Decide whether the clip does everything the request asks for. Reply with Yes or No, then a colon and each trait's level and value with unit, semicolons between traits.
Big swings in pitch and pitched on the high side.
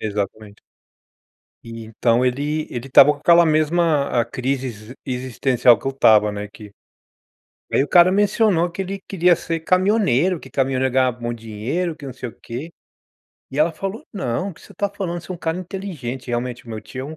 No: wide, 6.4 semitones; low, 135 Hz